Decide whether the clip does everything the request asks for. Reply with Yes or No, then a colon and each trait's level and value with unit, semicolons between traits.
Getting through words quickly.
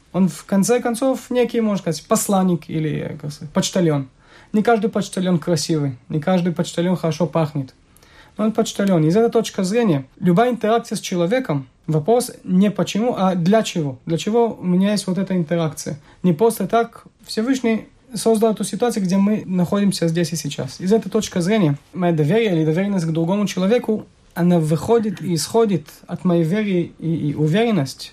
Yes: fast, 165 wpm